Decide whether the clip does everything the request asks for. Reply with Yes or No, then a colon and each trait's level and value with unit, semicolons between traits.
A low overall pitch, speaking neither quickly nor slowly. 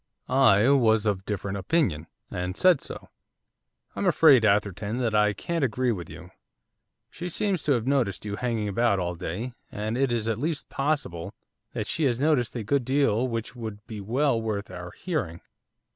Yes: low, 115 Hz; average, 180 wpm